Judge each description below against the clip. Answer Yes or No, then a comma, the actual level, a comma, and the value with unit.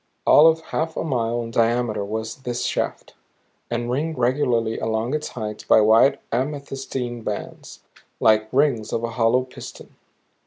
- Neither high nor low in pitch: No, low, 120 Hz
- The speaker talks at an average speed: Yes, average, 150 wpm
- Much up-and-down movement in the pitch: No, average, 3.2 semitones